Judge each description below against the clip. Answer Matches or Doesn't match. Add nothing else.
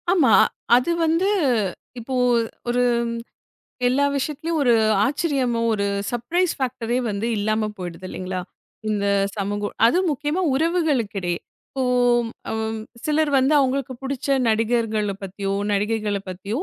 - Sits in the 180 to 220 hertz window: Doesn't match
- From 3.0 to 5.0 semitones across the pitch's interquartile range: Doesn't match